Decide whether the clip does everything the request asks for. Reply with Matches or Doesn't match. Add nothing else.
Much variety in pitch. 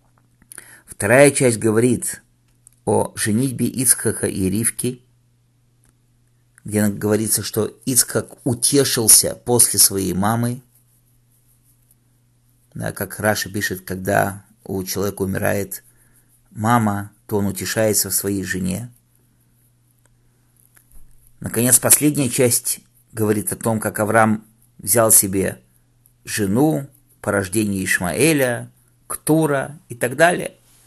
Doesn't match